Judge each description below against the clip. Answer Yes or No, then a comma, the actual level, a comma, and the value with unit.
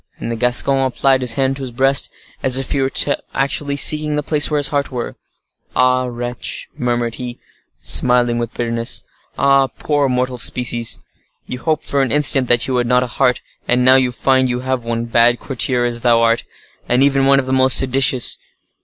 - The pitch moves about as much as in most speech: No, narrow, 1.9 semitones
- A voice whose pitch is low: Yes, low, 125 Hz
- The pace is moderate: Yes, average, 190 wpm